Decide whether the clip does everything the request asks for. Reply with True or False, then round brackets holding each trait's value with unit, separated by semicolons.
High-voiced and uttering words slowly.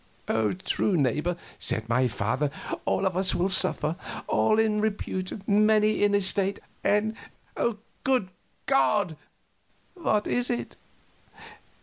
True (195 Hz; 115 wpm)